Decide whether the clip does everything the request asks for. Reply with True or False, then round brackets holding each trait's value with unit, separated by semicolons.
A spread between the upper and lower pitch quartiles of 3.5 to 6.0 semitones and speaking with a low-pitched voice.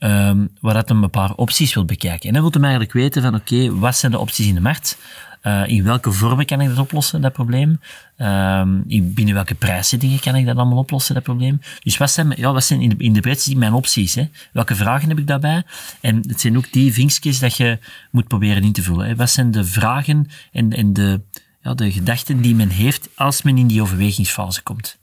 True (4.5 semitones; 120 Hz)